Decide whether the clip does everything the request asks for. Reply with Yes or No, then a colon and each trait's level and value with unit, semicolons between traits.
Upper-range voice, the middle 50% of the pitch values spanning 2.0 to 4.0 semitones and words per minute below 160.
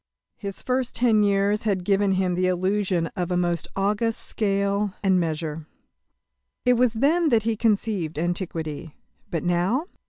Yes: high, 195 Hz; average, 3.6 semitones; average, 150 wpm